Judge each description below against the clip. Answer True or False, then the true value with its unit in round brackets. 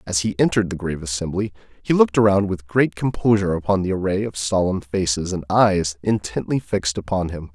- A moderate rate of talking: True (190 wpm)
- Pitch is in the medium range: False (95 Hz)